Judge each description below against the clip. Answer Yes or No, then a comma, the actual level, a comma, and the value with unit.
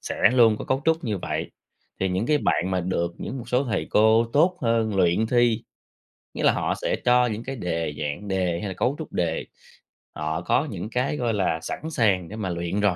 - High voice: No, low, 105 Hz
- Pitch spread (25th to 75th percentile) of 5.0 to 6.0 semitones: Yes, wide, 5.5 semitones